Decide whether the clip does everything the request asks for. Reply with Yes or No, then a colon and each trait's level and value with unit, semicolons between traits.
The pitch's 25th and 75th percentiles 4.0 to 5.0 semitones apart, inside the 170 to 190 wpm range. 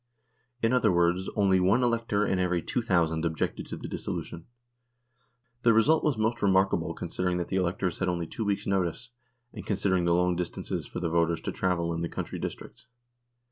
No: average, 3.4 semitones; average, 185 wpm